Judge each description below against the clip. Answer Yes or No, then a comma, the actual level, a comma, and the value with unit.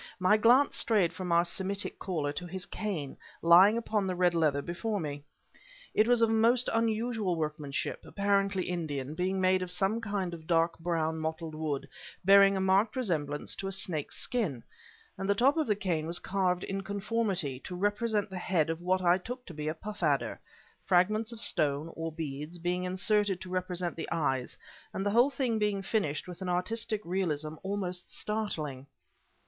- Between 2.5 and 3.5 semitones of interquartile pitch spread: No, average, 4.1 semitones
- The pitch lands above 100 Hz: Yes, medium, 185 Hz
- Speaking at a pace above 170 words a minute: Yes, average, 180 wpm